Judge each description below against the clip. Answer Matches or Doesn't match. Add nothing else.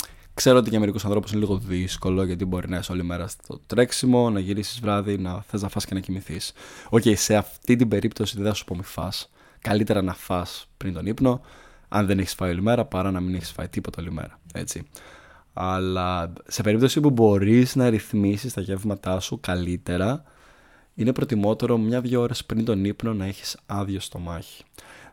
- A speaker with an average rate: Doesn't match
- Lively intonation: Doesn't match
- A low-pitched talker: Matches